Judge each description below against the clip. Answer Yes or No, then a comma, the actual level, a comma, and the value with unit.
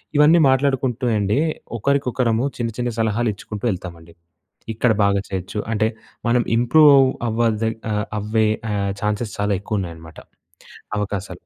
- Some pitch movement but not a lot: Yes, average, 3.5 semitones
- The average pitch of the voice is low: Yes, low, 110 Hz